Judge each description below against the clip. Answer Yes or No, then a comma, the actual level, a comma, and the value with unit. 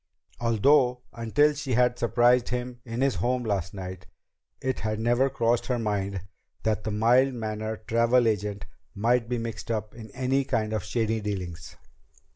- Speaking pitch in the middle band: No, low, 115 Hz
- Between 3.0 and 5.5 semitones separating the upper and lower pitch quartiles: No, narrow, 2.6 semitones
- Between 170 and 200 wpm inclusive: No, average, 160 wpm